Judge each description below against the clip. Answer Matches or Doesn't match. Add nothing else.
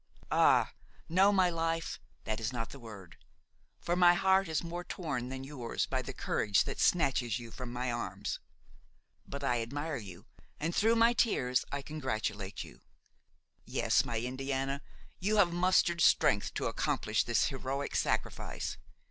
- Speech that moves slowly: Doesn't match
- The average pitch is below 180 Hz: Matches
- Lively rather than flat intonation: Matches